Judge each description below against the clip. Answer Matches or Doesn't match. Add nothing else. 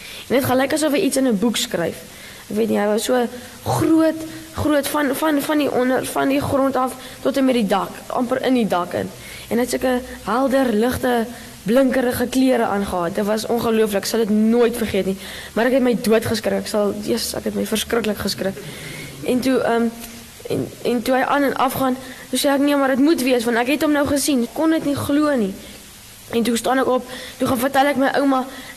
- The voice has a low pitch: Doesn't match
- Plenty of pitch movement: Doesn't match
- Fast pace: Matches